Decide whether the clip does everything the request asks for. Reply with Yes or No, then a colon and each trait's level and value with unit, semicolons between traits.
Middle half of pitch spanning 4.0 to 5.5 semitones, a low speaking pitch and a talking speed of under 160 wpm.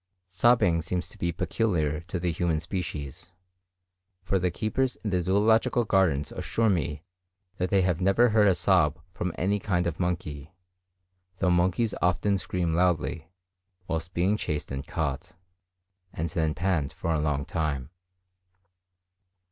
No: average, 3.4 semitones; very low, 90 Hz; average, 145 wpm